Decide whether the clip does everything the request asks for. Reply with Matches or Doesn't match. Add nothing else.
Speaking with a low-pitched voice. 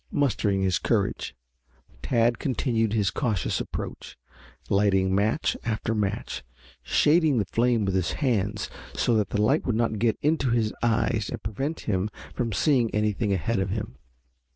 Matches